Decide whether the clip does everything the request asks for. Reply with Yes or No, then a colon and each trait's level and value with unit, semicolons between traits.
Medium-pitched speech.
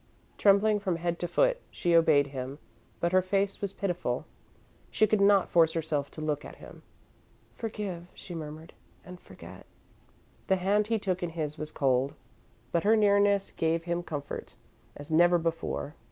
Yes: medium, 175 Hz